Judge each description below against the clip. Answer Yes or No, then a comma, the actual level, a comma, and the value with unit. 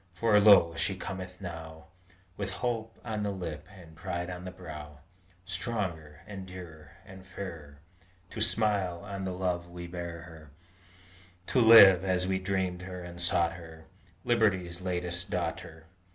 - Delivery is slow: No, average, 150 wpm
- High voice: No, very low, 90 Hz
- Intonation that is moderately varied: No, narrow, 2.2 semitones